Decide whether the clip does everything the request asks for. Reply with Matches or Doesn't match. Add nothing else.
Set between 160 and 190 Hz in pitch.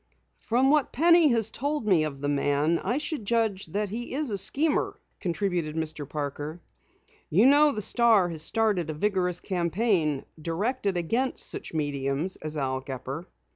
Matches